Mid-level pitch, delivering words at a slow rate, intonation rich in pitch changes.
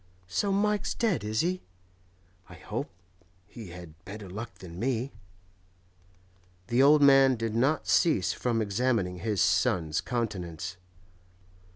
No: low, 115 Hz; slow, 120 wpm; wide, 6.6 semitones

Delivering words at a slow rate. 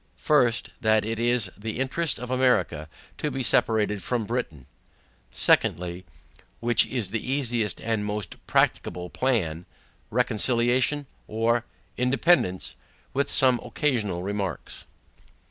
Yes: slow, 110 wpm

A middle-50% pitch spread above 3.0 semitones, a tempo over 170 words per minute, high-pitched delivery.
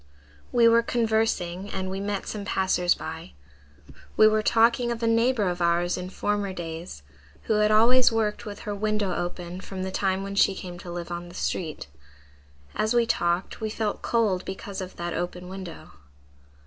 Yes: average, 3.5 semitones; average, 180 wpm; high, 195 Hz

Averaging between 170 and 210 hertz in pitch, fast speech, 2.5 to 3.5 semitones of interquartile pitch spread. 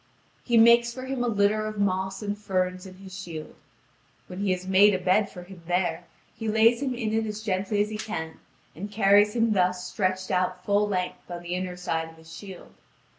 Yes: high, 195 Hz; fast, 215 wpm; average, 2.8 semitones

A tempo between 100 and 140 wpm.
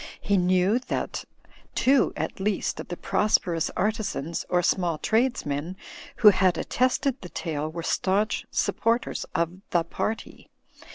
Yes: slow, 135 wpm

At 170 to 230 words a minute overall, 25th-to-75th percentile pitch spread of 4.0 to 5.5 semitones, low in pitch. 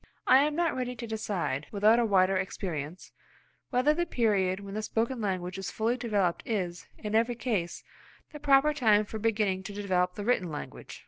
No: average, 185 wpm; average, 4.3 semitones; high, 210 Hz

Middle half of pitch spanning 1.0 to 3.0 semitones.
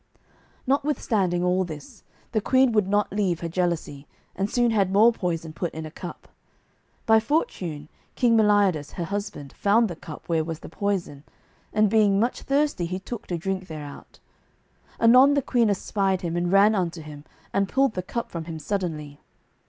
No: average, 4.6 semitones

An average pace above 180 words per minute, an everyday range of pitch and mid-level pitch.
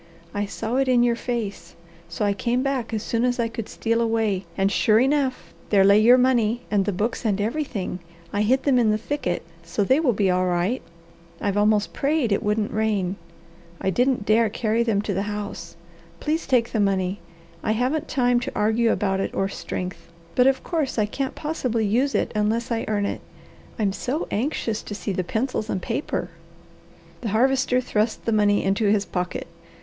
No: average, 195 wpm; average, 3.4 semitones; high, 220 Hz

